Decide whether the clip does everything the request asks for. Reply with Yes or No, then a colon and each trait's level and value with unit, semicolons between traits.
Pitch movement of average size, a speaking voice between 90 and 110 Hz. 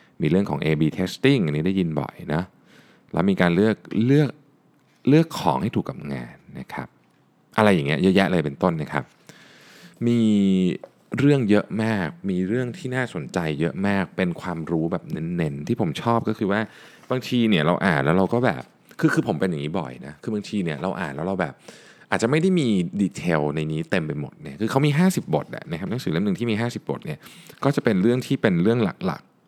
No: wide, 6.7 semitones; low, 105 Hz